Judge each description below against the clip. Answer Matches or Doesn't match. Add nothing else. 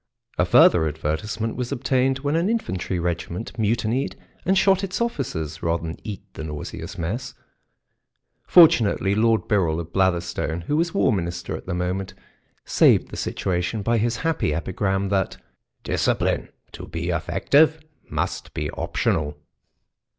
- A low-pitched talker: Matches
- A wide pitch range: Matches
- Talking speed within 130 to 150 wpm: Matches